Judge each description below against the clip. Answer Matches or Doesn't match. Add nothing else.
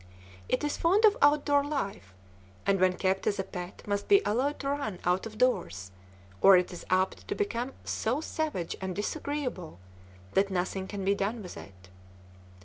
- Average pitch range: Doesn't match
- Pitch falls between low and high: Doesn't match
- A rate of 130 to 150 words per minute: Doesn't match